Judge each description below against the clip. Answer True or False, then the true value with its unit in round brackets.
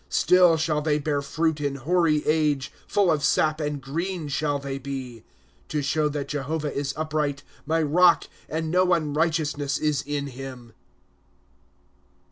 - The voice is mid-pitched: True (150 Hz)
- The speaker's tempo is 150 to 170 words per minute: True (155 wpm)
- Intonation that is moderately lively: False (2.2 semitones)